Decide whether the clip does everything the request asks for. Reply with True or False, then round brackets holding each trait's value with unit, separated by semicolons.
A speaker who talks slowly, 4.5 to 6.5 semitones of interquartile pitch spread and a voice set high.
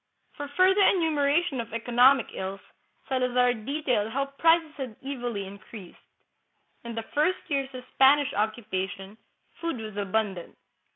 True (130 wpm; 4.9 semitones; 250 Hz)